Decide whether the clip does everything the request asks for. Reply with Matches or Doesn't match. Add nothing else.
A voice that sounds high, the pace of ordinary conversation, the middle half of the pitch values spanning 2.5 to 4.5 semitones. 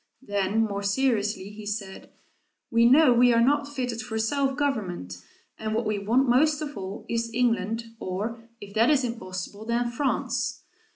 Matches